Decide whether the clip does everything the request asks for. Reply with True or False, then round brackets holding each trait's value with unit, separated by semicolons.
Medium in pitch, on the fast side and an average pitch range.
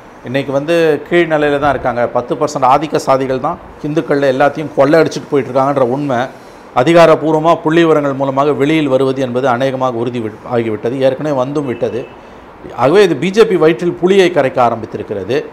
True (145 Hz; 140 wpm; 3.0 semitones)